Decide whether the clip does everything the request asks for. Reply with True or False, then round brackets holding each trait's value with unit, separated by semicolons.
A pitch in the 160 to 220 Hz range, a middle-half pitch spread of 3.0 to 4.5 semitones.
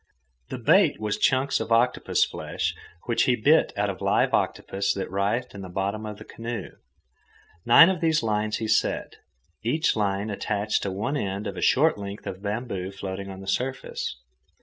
False (105 Hz; 3.6 semitones)